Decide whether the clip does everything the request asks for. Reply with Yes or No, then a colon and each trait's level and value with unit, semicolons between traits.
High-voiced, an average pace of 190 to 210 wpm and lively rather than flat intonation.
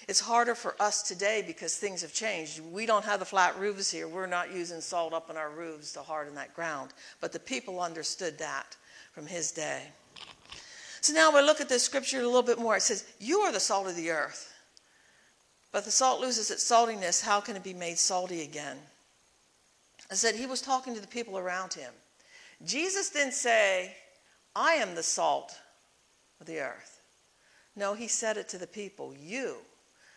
Yes: high, 205 Hz; average, 195 wpm; wide, 5.9 semitones